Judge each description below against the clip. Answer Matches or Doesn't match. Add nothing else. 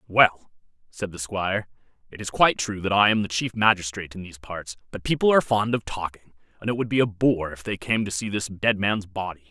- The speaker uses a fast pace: Matches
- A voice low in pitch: Matches